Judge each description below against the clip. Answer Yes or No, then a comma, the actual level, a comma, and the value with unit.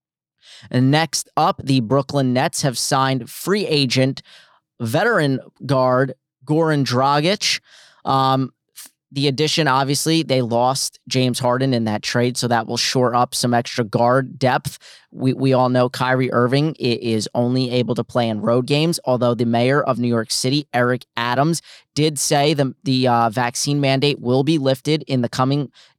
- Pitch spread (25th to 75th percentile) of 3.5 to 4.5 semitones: No, narrow, 2.6 semitones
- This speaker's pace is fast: No, average, 160 wpm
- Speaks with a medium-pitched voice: No, low, 130 Hz